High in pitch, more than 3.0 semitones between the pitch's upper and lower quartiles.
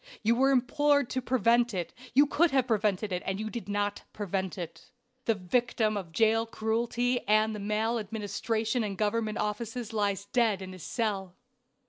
No: high, 220 Hz; average, 2.7 semitones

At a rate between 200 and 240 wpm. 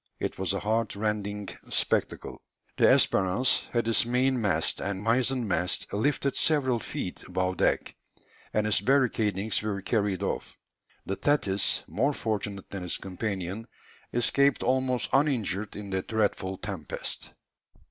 No: slow, 135 wpm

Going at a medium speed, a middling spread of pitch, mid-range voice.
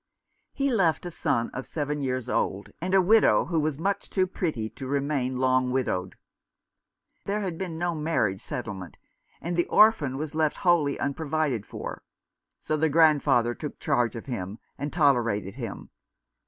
Yes: average, 160 wpm; average, 5.0 semitones; medium, 145 Hz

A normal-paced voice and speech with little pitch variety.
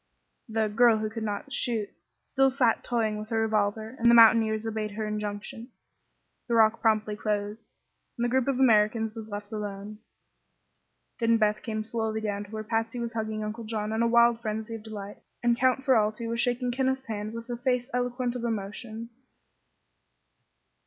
Yes: average, 175 wpm; narrow, 1.8 semitones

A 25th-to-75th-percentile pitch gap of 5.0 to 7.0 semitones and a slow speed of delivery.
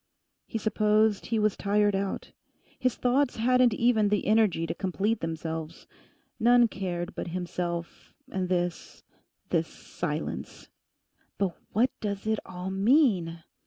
No: average, 4.0 semitones; slow, 125 wpm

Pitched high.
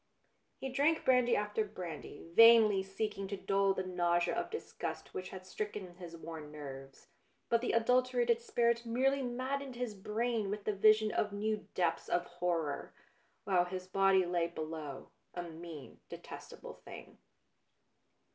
Yes: high, 195 Hz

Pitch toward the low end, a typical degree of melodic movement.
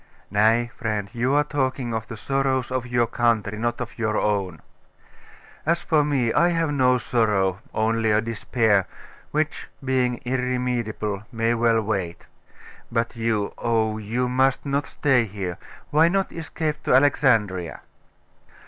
Yes: low, 120 Hz; average, 3.4 semitones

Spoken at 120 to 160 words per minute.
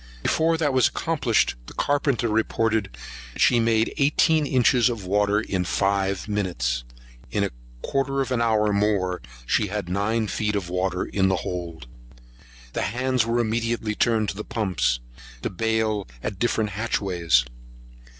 Yes: average, 150 wpm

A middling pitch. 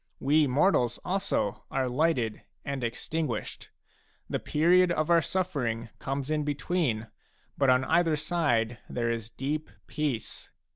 Yes: medium, 145 Hz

